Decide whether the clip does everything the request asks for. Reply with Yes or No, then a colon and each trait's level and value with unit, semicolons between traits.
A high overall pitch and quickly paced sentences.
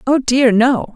No: very high, 250 Hz; average, 190 wpm